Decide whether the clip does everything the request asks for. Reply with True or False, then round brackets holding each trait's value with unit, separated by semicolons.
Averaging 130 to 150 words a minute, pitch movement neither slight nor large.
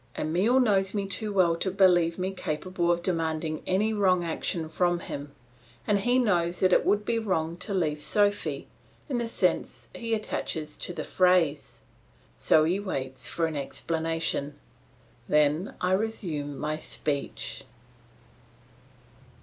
True (140 wpm; 4.1 semitones)